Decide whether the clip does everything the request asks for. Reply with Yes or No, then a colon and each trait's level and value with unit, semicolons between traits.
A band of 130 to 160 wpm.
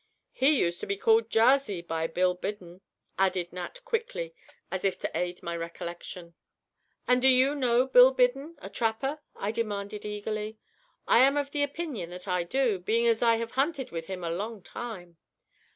No: average, 180 wpm